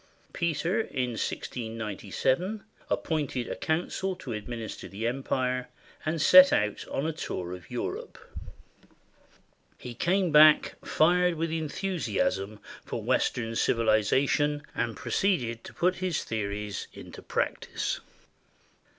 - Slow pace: Yes, slow, 115 wpm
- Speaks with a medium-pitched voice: No, low, 130 Hz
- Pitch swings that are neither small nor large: No, wide, 6.9 semitones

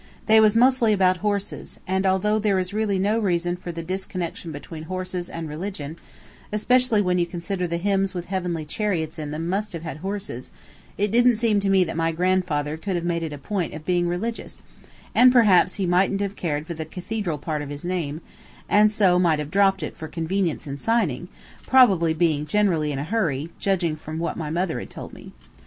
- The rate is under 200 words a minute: No, fast, 205 wpm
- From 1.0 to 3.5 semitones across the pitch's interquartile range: No, average, 3.9 semitones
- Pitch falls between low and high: Yes, medium, 180 Hz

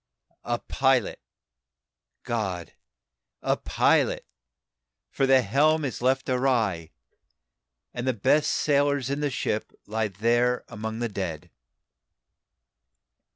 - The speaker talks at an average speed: No, slow, 105 wpm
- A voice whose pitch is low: Yes, low, 120 Hz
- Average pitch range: Yes, average, 3.8 semitones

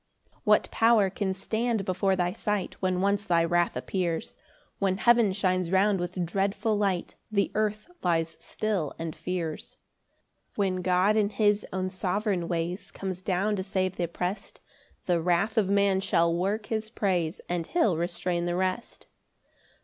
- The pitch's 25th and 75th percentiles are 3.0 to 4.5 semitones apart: No, narrow, 2.6 semitones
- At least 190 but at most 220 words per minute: No, average, 160 wpm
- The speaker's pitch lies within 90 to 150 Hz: No, high, 190 Hz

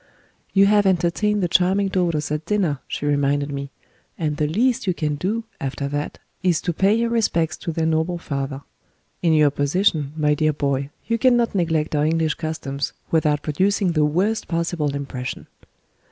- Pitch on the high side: No, medium, 160 Hz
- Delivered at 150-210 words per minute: Yes, average, 170 wpm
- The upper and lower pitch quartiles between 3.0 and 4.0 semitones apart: No, average, 4.4 semitones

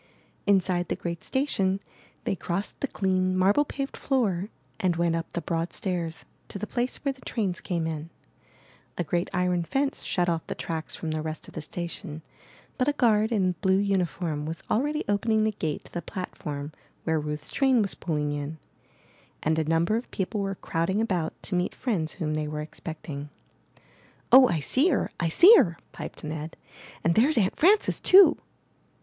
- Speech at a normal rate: Yes, average, 180 wpm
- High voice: No, medium, 180 Hz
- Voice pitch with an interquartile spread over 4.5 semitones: Yes, average, 5.1 semitones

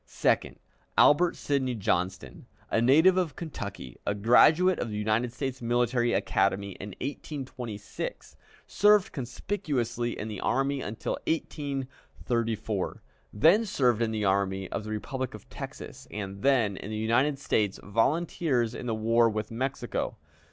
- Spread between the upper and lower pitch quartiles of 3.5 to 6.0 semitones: Yes, average, 4.5 semitones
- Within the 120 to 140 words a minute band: Yes, slow, 135 wpm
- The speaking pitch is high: No, low, 120 Hz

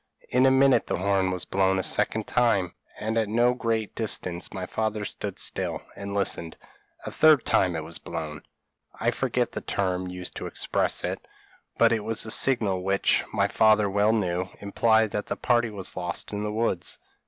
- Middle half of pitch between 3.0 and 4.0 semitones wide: Yes, average, 3.3 semitones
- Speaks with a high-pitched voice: No, low, 105 Hz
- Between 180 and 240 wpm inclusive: Yes, average, 190 wpm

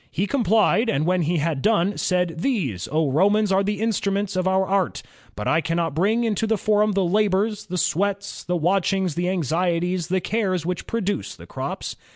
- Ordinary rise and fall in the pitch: Yes, average, 3.3 semitones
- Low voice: No, high, 190 Hz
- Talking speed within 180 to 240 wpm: Yes, average, 185 wpm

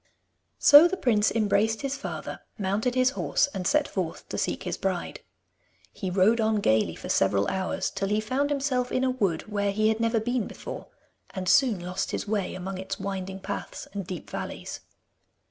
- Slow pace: No, average, 185 wpm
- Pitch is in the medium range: No, high, 210 Hz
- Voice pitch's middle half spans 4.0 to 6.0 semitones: Yes, average, 4.5 semitones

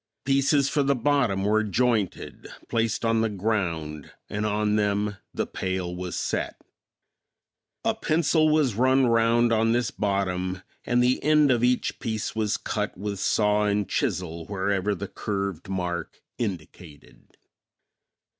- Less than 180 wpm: Yes, slow, 135 wpm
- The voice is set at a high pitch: No, low, 105 Hz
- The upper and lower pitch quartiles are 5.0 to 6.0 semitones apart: No, average, 4.0 semitones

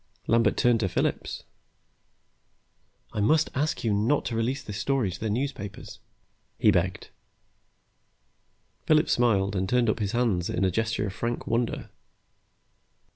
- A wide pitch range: No, average, 3.3 semitones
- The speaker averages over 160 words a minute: No, average, 140 wpm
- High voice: No, low, 115 Hz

